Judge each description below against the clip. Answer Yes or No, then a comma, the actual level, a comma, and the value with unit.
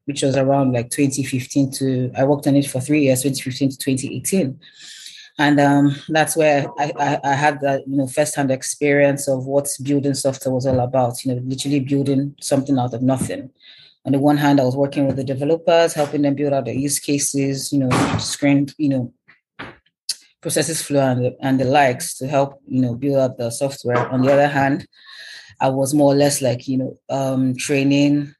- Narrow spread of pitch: Yes, narrow, 1.4 semitones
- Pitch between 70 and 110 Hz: No, medium, 140 Hz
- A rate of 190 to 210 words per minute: Yes, average, 200 wpm